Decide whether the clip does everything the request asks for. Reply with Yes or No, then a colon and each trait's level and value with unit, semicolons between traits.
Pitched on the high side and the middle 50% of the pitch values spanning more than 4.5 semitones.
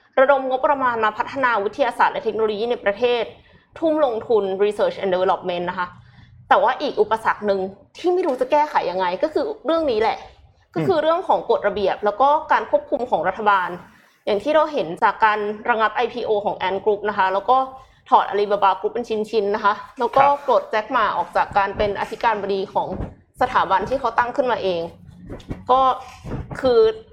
Yes: high, 220 Hz; average, 4.9 semitones